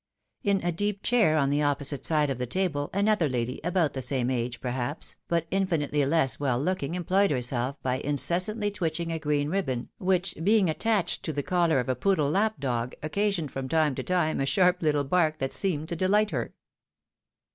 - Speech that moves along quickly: No, average, 190 wpm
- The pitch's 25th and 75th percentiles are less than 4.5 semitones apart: No, average, 5.3 semitones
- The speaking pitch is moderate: Yes, medium, 155 Hz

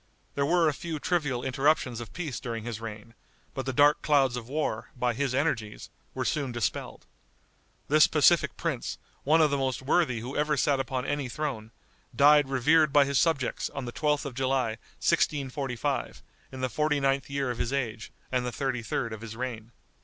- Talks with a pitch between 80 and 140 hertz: Yes, low, 135 Hz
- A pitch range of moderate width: Yes, average, 3.4 semitones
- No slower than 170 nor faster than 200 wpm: Yes, average, 190 wpm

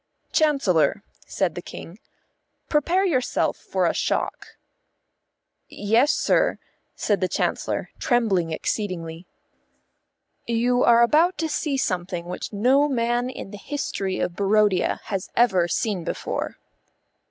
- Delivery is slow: Yes, slow, 120 wpm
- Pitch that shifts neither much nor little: No, wide, 6.0 semitones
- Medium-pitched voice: No, high, 215 Hz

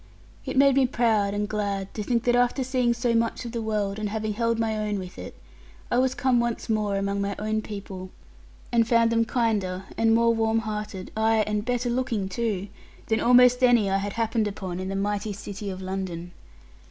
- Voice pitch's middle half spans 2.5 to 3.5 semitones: Yes, average, 2.8 semitones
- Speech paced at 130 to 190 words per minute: No, fast, 205 wpm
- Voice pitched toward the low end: No, high, 220 Hz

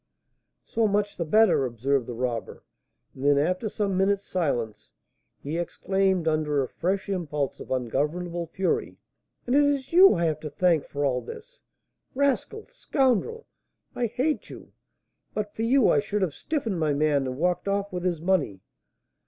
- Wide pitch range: Yes, wide, 6.6 semitones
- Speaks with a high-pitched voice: No, medium, 180 Hz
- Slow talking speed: No, average, 165 wpm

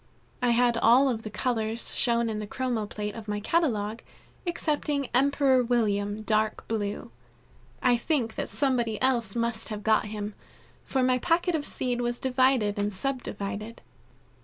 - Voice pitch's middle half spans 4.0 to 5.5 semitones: No, average, 3.3 semitones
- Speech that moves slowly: No, average, 160 wpm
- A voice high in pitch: Yes, high, 235 Hz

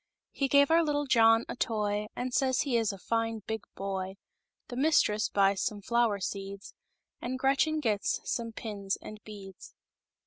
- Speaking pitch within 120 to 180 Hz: No, high, 225 Hz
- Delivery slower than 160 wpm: Yes, average, 140 wpm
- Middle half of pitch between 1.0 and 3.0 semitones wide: No, average, 4.3 semitones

